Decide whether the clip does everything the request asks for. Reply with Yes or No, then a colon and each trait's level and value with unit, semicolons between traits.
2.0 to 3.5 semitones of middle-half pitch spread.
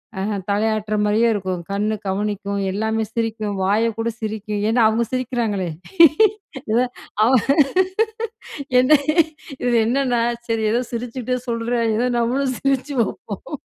Yes: narrow, 2.6 semitones